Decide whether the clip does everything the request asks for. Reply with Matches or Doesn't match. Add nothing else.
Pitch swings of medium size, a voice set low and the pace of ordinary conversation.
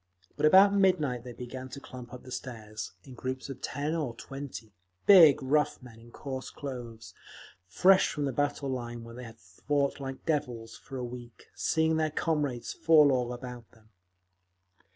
Matches